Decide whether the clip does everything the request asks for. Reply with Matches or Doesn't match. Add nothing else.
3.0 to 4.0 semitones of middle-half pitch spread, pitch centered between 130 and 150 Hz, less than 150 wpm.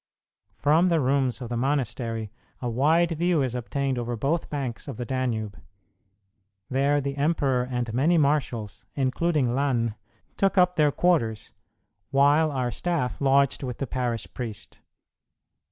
Matches